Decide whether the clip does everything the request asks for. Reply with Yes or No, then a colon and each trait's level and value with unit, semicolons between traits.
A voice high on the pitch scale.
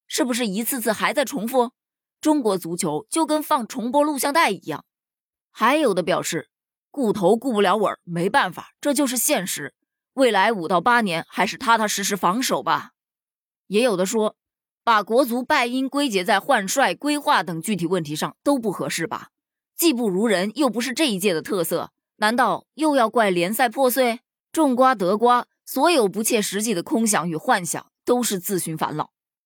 Yes: high, 240 Hz